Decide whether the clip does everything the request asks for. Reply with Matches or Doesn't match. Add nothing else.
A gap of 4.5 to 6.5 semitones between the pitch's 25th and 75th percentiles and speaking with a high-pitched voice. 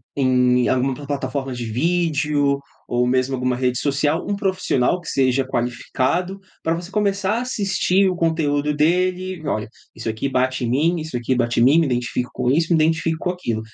Doesn't match